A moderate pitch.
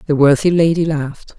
Yes: medium, 155 Hz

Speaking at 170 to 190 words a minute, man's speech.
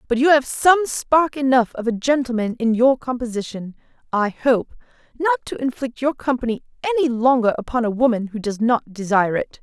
No: average, 180 wpm; female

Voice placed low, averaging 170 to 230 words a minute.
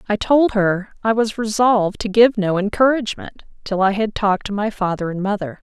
No: high, 205 Hz; average, 200 wpm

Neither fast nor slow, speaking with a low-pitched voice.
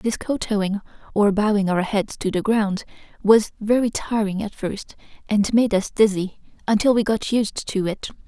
No: average, 175 wpm; high, 210 Hz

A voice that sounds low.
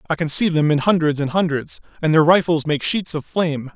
No: medium, 160 Hz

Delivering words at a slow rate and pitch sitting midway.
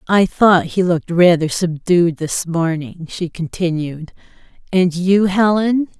Yes: slow, 130 wpm; medium, 175 Hz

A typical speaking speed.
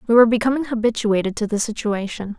Yes: average, 175 wpm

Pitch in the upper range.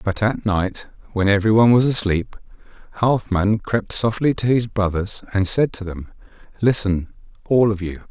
No: low, 105 Hz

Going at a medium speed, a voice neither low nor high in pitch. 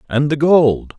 Yes: average, 180 wpm; medium, 145 Hz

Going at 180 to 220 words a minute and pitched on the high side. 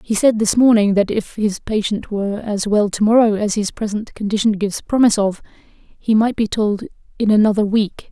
Yes: average, 200 wpm; high, 210 Hz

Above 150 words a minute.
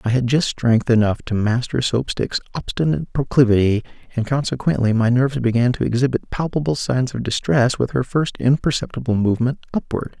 Yes: average, 165 wpm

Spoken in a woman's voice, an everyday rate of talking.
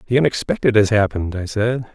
No: male; average, 185 wpm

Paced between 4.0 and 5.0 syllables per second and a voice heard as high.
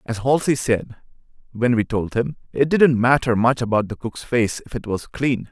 No: 4.6 syllables/s; low, 120 Hz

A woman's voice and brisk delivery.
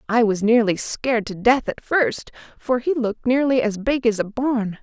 Yes: female; fast, 210 wpm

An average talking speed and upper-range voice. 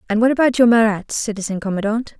Yes: average, 190 wpm; high, 220 Hz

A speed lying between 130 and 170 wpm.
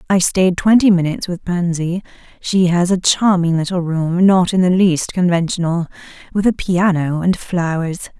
Yes: average, 160 wpm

